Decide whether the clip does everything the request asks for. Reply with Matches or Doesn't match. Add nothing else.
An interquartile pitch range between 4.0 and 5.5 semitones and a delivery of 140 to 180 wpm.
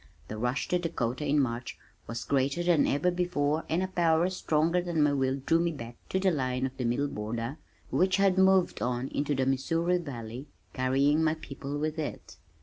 Doesn't match